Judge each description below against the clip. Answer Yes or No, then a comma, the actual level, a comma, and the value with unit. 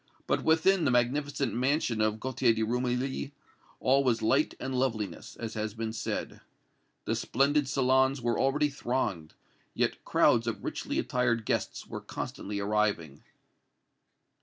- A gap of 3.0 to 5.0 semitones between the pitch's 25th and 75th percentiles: Yes, average, 3.7 semitones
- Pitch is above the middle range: No, low, 125 Hz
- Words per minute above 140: No, slow, 135 wpm